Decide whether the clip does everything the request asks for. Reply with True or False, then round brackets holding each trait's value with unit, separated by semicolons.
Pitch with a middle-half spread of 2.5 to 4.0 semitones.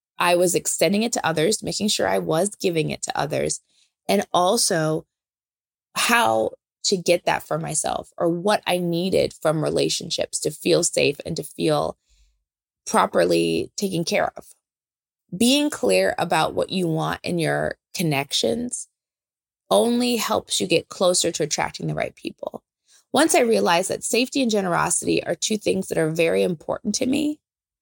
False (5.1 semitones)